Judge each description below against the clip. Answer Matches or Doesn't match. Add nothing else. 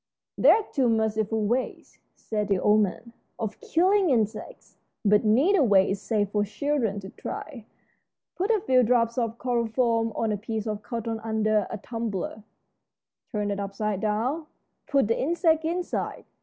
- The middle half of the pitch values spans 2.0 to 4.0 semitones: Matches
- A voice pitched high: Matches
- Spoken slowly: Doesn't match